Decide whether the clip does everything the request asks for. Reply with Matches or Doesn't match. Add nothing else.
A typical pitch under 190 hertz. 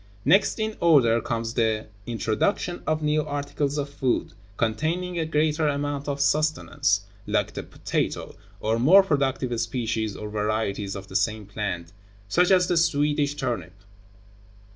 Matches